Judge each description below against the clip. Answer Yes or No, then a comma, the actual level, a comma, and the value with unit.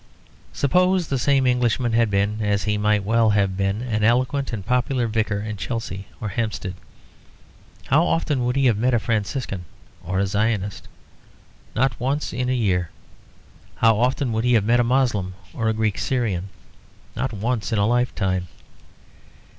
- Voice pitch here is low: Yes, low, 110 Hz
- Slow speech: No, average, 165 wpm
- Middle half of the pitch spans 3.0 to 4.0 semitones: Yes, average, 3.5 semitones